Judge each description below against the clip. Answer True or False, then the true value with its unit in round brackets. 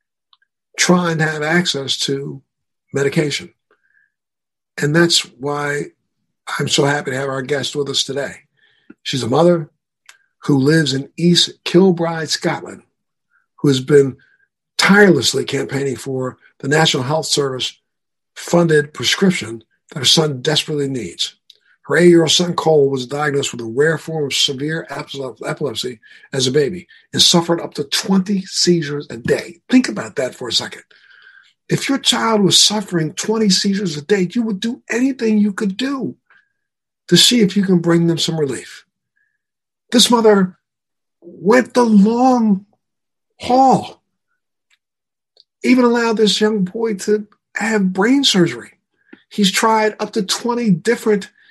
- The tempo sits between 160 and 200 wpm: False (145 wpm)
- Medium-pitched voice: True (175 Hz)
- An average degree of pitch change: False (6.7 semitones)